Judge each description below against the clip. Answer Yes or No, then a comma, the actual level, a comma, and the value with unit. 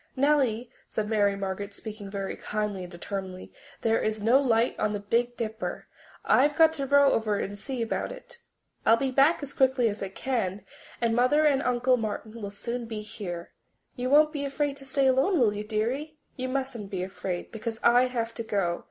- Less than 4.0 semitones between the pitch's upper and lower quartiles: No, average, 4.4 semitones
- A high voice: Yes, high, 230 Hz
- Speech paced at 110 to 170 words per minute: No, average, 200 wpm